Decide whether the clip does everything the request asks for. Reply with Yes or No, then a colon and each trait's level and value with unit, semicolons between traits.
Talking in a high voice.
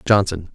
No: very low, 95 Hz